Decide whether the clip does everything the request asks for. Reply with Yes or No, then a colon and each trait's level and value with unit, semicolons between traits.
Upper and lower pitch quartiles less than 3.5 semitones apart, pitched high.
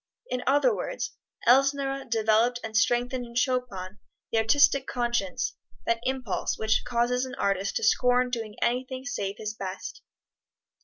Yes: average, 2.9 semitones; high, 240 Hz